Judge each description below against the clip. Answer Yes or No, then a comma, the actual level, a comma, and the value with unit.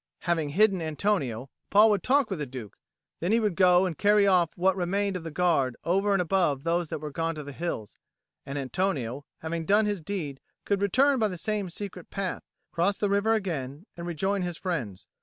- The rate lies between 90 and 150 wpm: No, fast, 205 wpm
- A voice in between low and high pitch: Yes, medium, 180 Hz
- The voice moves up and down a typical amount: Yes, average, 4.5 semitones